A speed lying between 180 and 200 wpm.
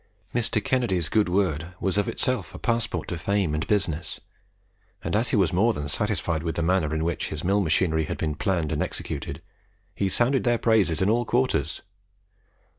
Yes: average, 190 wpm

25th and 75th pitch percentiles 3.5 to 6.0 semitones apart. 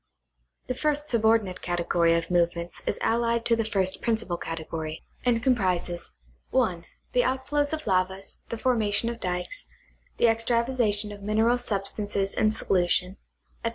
Yes: average, 4.6 semitones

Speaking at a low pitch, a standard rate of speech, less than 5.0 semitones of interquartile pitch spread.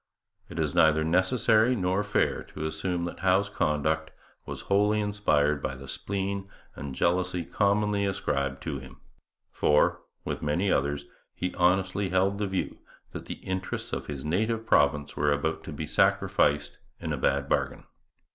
No: very low, 90 Hz; average, 155 wpm; average, 5.3 semitones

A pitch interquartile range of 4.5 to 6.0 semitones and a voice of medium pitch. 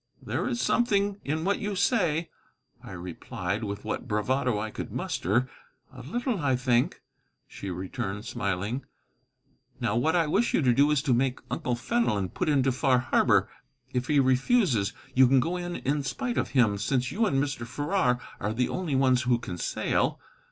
No: wide, 5.5 semitones; low, 130 Hz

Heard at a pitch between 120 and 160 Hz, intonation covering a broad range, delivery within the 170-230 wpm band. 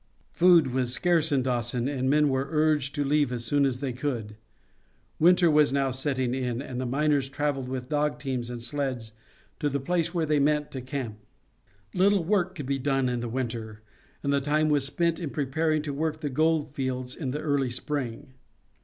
No: medium, 140 Hz; average, 3.0 semitones; average, 200 wpm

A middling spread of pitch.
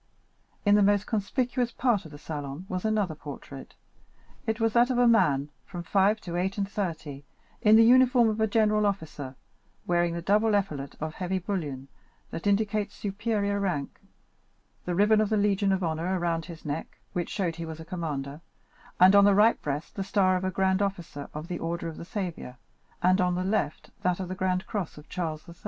Yes: average, 4.0 semitones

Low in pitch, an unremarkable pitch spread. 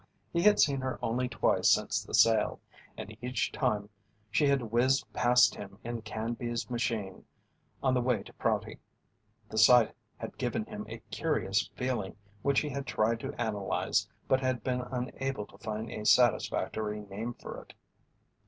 Yes: low, 120 Hz; average, 3.0 semitones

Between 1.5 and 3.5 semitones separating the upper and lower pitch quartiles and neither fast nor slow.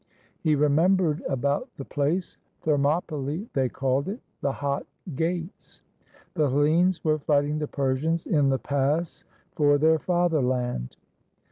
No: average, 2.8 semitones; slow, 130 wpm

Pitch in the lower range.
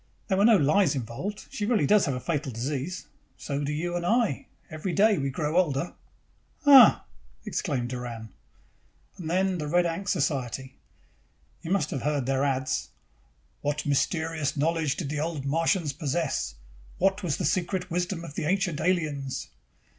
No: medium, 155 Hz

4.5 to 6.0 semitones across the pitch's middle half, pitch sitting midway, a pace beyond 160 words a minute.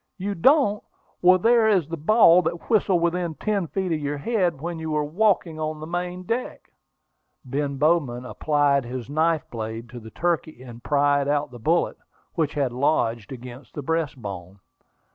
Yes: average, 4.8 semitones; medium, 155 Hz; average, 170 wpm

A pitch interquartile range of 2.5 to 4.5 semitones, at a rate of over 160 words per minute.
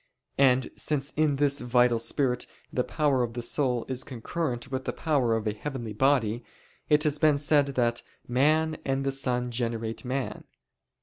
Yes: average, 3.0 semitones; average, 170 wpm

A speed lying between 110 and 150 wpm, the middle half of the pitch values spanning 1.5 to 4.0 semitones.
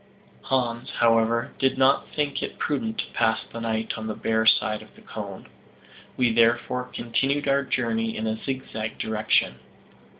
No: average, 160 wpm; average, 2.9 semitones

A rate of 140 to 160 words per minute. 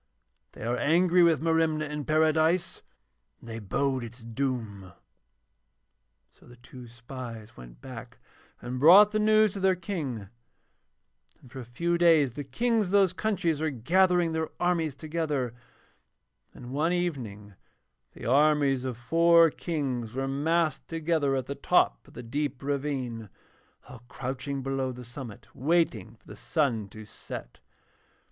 Yes: average, 145 wpm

